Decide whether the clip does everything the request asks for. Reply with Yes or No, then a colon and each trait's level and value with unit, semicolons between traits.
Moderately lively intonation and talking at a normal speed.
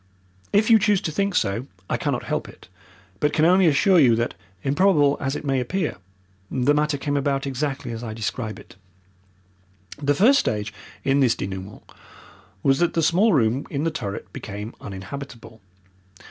No: wide, 5.9 semitones; average, 170 wpm